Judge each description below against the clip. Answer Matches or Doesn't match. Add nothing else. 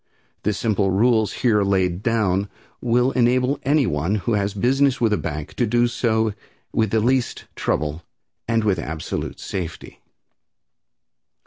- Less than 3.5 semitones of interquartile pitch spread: Doesn't match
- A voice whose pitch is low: Matches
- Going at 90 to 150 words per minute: Matches